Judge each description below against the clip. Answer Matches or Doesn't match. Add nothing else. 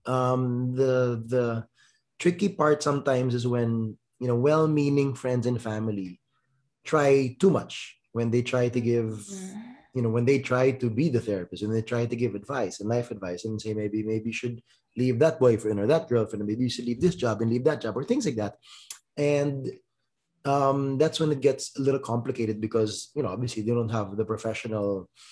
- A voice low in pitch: Matches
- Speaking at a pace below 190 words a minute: Doesn't match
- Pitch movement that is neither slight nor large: Matches